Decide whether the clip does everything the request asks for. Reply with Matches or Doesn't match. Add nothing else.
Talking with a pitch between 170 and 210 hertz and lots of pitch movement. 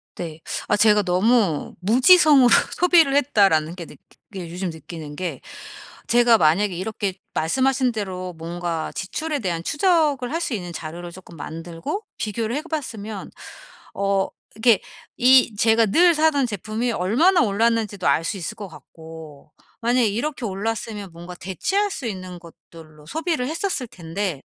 Matches